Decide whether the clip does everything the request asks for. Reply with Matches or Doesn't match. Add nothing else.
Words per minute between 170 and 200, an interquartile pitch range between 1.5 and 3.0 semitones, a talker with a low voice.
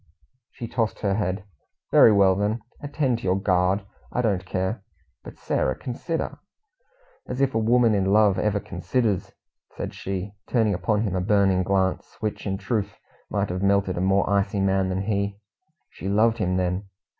Matches